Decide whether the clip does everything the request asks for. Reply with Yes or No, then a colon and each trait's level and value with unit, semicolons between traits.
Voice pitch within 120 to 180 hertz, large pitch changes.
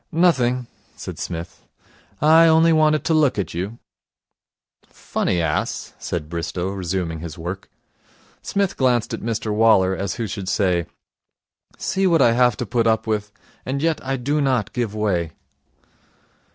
No: low, 110 Hz; wide, 6.9 semitones